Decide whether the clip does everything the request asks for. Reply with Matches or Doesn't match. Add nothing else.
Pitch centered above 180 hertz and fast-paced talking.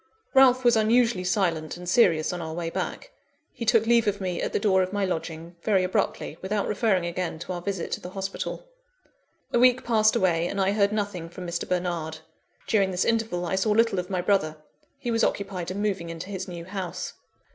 Matches